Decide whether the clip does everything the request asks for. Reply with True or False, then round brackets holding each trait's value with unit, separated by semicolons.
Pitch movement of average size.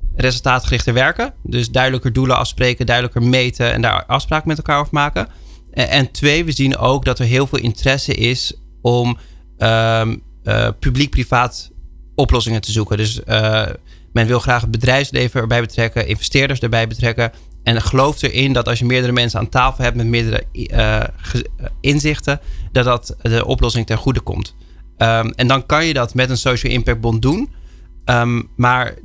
False (2.3 semitones)